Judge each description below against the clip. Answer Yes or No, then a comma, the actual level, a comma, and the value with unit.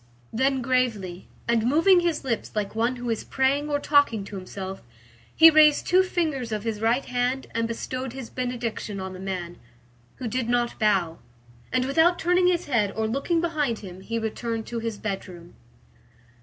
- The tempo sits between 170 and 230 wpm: Yes, average, 175 wpm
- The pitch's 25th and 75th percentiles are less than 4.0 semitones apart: No, average, 4.6 semitones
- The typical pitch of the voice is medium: No, high, 240 Hz